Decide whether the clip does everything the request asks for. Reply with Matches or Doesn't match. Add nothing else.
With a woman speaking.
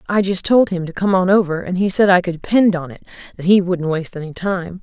Matches